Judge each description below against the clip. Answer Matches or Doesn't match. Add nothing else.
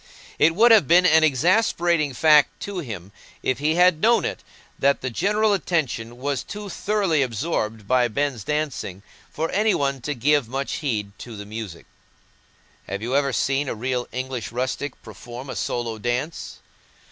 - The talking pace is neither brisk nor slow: Matches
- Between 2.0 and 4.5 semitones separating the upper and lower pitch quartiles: Doesn't match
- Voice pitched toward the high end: Doesn't match